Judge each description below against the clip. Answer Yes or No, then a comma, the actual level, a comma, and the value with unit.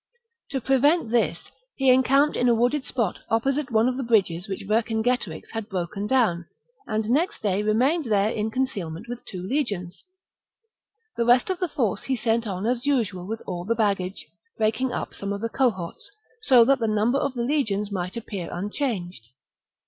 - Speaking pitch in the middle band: No, high, 225 Hz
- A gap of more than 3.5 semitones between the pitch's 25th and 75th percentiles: Yes, average, 4.4 semitones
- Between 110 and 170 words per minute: No, average, 185 wpm